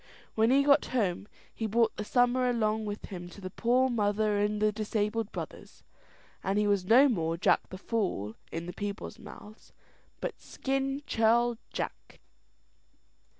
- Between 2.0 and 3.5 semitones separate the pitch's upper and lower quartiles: Yes, average, 2.8 semitones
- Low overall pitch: No, high, 215 Hz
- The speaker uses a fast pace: No, average, 155 wpm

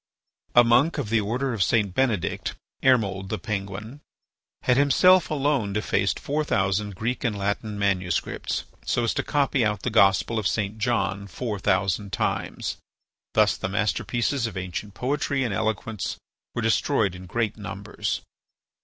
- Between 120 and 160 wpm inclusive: Yes, average, 150 wpm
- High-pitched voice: No, low, 110 Hz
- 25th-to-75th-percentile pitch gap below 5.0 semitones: Yes, average, 3.7 semitones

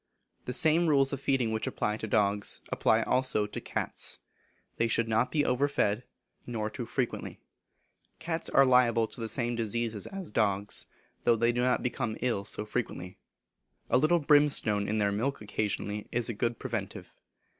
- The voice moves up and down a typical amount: Yes, average, 3.7 semitones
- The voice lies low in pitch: Yes, low, 120 Hz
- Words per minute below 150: No, average, 170 wpm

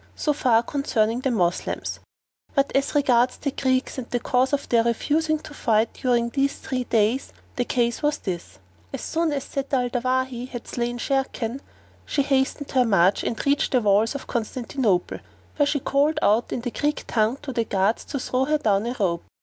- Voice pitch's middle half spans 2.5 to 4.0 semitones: Yes, average, 3.3 semitones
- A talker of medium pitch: No, very high, 250 Hz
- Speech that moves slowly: No, average, 190 wpm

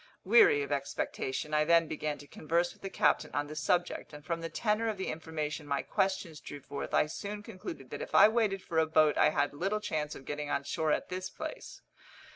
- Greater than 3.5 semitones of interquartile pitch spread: Yes, average, 4.1 semitones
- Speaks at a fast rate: Yes, fast, 225 wpm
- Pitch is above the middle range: No, medium, 160 Hz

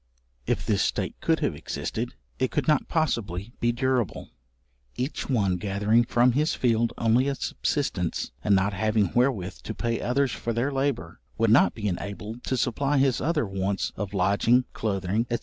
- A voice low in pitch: Yes, low, 115 Hz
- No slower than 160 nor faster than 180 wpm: Yes, average, 170 wpm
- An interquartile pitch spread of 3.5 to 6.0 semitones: Yes, average, 4.2 semitones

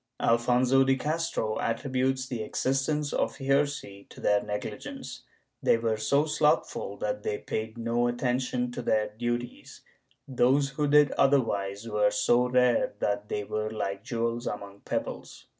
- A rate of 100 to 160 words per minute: Yes, average, 140 wpm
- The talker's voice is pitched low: Yes, low, 120 Hz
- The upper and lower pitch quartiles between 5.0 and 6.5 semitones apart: No, average, 3.7 semitones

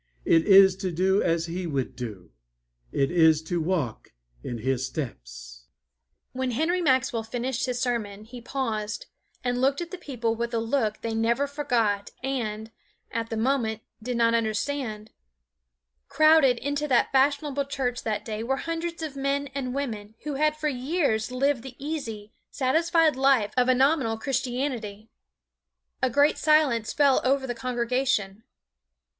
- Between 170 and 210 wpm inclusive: No, average, 150 wpm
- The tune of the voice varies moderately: Yes, average, 4.7 semitones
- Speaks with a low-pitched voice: No, high, 245 Hz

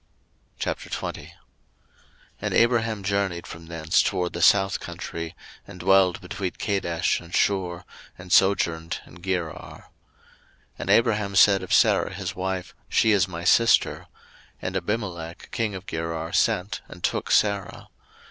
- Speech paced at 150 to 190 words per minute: No, slow, 135 wpm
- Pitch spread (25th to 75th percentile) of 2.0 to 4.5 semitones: Yes, average, 2.7 semitones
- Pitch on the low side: Yes, very low, 95 Hz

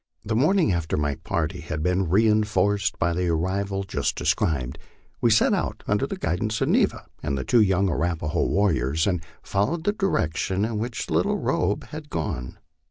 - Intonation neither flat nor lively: Yes, average, 4.7 semitones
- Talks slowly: No, average, 175 wpm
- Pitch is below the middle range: Yes, very low, 95 Hz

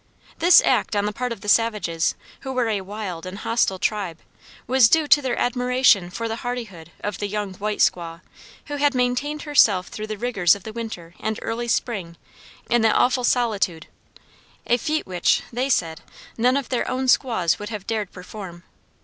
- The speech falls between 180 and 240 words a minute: Yes, average, 185 wpm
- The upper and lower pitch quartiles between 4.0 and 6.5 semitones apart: Yes, average, 4.6 semitones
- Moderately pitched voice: No, high, 220 Hz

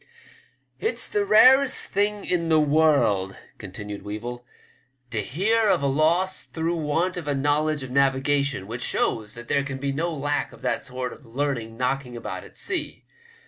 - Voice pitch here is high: No, medium, 140 Hz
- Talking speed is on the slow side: No, average, 175 wpm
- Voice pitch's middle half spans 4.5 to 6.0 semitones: Yes, average, 5.1 semitones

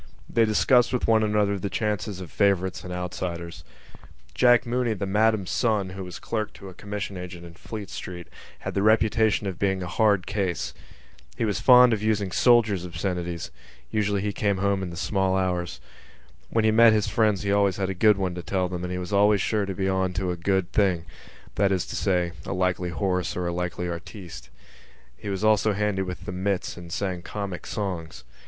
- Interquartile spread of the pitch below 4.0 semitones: Yes, average, 2.8 semitones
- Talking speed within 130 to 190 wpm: No, average, 200 wpm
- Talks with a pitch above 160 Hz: No, very low, 95 Hz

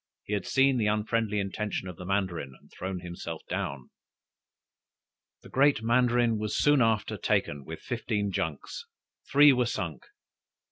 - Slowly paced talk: No, average, 145 wpm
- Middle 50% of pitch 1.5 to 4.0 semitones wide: No, average, 4.7 semitones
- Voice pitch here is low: Yes, low, 105 Hz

